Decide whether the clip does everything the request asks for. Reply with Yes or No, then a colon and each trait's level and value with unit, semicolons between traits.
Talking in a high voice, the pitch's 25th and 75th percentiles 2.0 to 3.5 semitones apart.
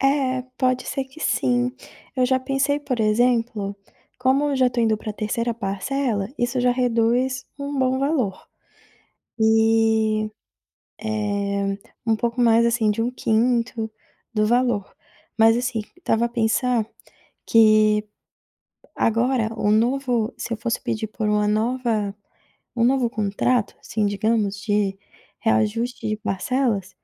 Yes: high, 230 Hz; average, 2.9 semitones